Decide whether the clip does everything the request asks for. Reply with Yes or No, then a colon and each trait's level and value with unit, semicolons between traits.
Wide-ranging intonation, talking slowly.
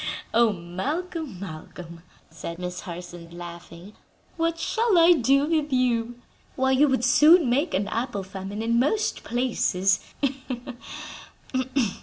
Yes: wide, 8.4 semitones; slow, 120 wpm